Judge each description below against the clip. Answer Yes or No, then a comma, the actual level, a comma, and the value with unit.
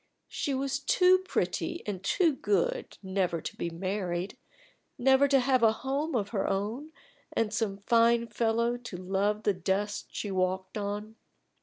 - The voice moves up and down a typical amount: Yes, average, 4.9 semitones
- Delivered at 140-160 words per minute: Yes, average, 155 wpm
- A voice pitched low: No, high, 215 Hz